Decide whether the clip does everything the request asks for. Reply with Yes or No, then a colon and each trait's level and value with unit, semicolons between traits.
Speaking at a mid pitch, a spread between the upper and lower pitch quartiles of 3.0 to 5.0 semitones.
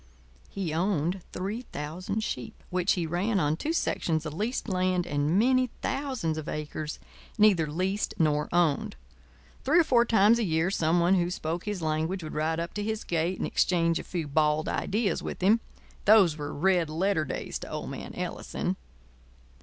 Yes: medium, 175 Hz; average, 4.6 semitones